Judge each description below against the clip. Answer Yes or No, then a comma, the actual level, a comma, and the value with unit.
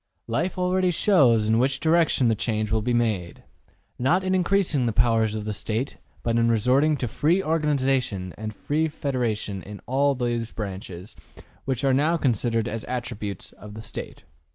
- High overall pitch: No, low, 120 Hz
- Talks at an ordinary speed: Yes, average, 170 wpm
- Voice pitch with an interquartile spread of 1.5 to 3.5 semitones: No, average, 5.2 semitones